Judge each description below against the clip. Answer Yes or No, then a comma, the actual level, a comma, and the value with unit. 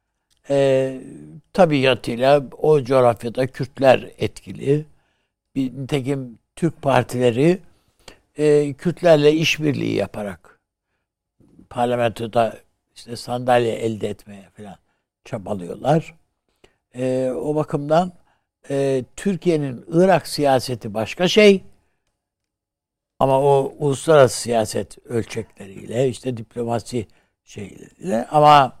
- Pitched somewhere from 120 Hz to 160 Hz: Yes, low, 135 Hz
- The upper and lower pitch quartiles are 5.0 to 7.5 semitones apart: No, average, 4.0 semitones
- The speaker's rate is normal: No, slow, 80 wpm